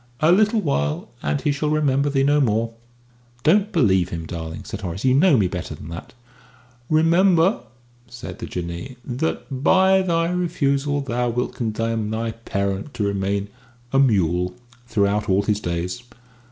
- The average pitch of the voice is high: No, low, 120 Hz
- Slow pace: No, average, 155 wpm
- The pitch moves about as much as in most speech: No, wide, 7.4 semitones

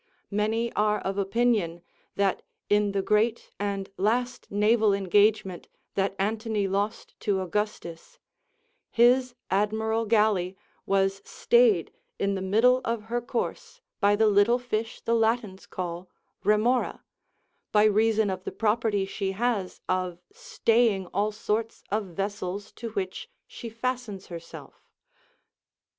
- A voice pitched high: Yes, high, 210 Hz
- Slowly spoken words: Yes, slow, 125 wpm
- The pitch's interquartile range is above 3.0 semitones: No, average, 2.7 semitones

